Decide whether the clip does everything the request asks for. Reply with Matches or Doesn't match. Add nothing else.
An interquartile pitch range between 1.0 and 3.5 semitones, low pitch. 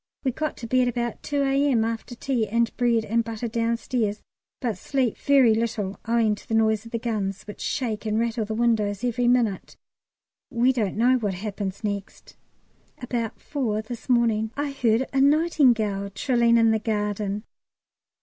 Doesn't match